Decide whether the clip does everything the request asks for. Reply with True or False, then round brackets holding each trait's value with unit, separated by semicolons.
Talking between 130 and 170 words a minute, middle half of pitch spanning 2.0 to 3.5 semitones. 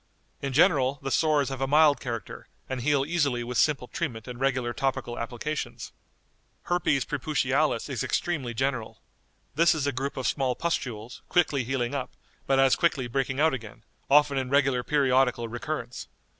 True (160 wpm; 2.8 semitones)